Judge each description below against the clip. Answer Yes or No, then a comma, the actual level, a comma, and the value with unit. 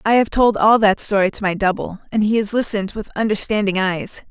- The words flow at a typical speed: No, fast, 225 wpm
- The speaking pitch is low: No, high, 205 Hz